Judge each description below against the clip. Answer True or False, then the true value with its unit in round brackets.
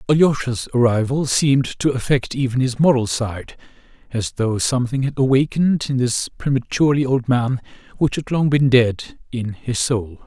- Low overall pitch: True (125 Hz)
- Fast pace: False (160 wpm)